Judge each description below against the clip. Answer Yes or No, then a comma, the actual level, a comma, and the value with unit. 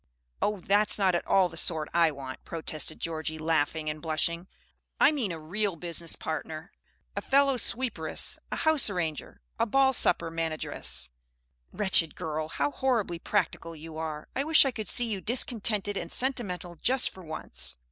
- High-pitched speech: No, medium, 175 Hz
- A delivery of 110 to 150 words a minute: No, average, 165 wpm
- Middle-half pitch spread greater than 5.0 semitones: Yes, wide, 5.4 semitones